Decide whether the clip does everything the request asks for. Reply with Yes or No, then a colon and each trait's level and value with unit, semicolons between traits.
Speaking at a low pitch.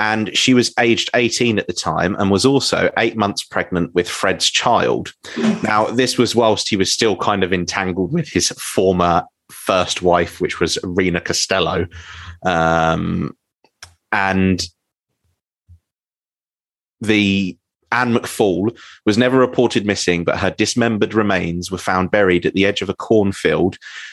Yes: very low, 95 Hz